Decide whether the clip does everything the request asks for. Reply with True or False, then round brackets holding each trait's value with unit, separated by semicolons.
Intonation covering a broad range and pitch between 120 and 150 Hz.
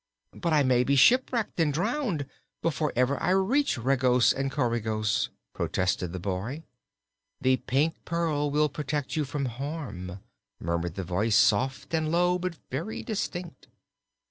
True (5.8 semitones; 140 Hz)